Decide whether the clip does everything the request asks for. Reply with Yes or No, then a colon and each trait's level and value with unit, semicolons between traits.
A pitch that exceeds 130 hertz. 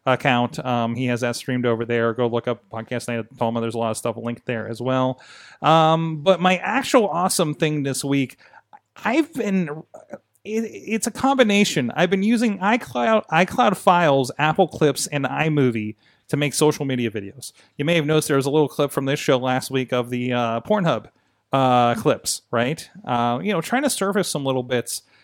Yes: medium, 140 Hz